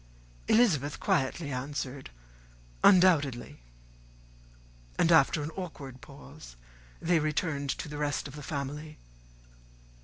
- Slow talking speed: Yes, slow, 100 wpm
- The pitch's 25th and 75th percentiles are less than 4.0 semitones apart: Yes, average, 2.9 semitones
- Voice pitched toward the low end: No, medium, 145 Hz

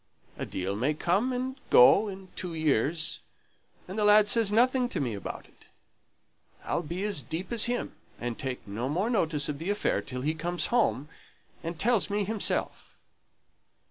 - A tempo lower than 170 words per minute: No, average, 175 wpm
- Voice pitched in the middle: Yes, medium, 175 Hz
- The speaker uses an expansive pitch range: Yes, wide, 6.4 semitones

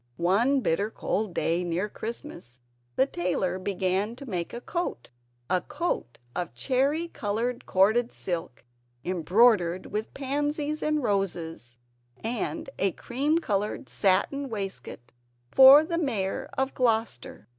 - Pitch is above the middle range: Yes, high, 210 Hz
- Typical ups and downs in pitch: No, wide, 6.8 semitones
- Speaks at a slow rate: Yes, slow, 125 wpm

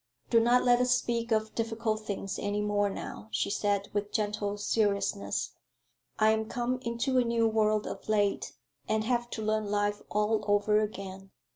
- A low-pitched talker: No, high, 215 Hz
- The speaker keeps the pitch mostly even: Yes, narrow, 2.0 semitones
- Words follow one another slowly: No, average, 170 wpm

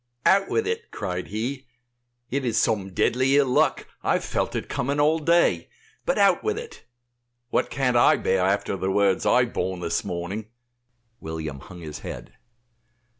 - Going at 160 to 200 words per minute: Yes, average, 175 wpm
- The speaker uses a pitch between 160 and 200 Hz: No, low, 115 Hz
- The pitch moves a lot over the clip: Yes, wide, 7.0 semitones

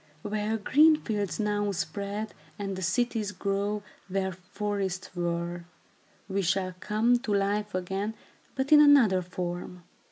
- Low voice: No, high, 200 Hz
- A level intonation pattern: Yes, narrow, 2.3 semitones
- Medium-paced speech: No, slow, 130 wpm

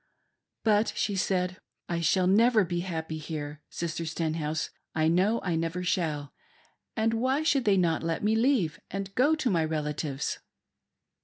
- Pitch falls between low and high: Yes, medium, 175 Hz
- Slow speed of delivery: No, average, 160 wpm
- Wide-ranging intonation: No, average, 4.9 semitones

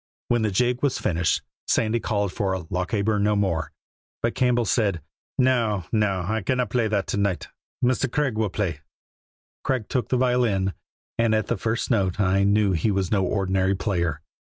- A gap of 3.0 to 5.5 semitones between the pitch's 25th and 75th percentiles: Yes, average, 3.6 semitones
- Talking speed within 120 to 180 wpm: Yes, average, 175 wpm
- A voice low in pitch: Yes, low, 105 Hz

